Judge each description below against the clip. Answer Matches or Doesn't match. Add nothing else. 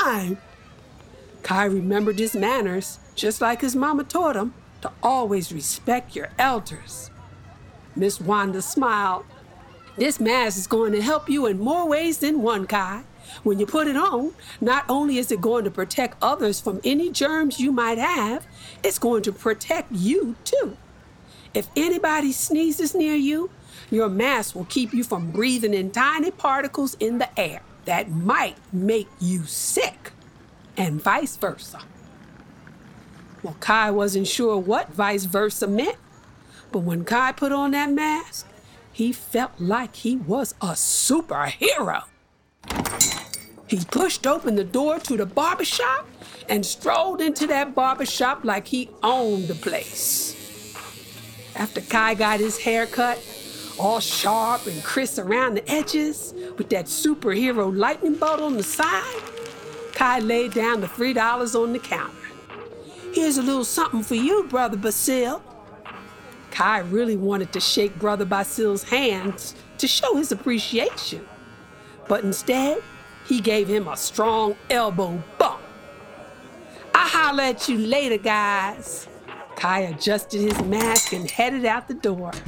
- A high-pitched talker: Matches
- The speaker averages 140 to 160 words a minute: Matches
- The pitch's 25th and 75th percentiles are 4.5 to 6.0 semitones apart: Matches